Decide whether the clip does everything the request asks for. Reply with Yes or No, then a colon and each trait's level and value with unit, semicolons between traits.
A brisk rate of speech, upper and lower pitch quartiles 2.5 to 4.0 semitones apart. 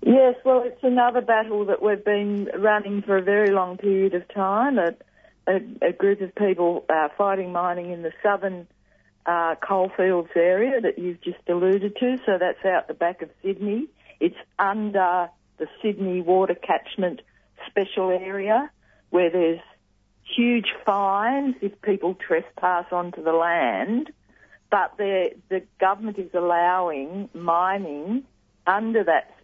No: average, 140 wpm; average, 2.9 semitones